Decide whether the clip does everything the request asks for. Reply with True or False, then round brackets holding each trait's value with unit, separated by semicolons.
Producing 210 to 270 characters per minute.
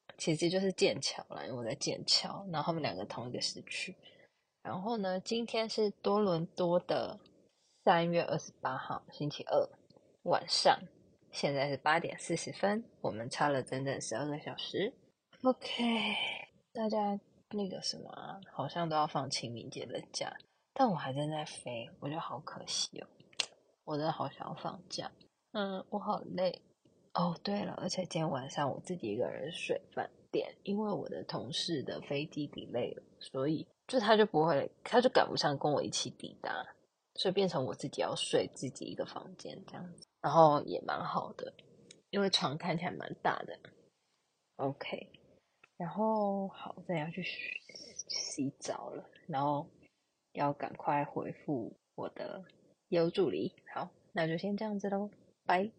True (240 characters per minute)